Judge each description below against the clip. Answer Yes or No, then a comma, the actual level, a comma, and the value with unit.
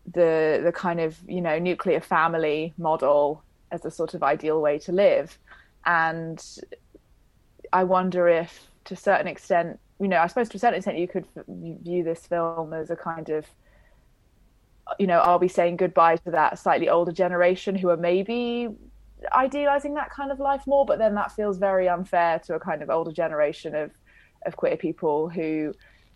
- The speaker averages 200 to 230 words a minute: No, average, 180 wpm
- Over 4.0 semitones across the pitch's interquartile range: No, average, 2.9 semitones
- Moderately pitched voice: Yes, medium, 170 Hz